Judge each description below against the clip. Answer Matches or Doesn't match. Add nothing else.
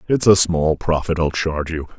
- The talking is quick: Matches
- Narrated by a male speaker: Matches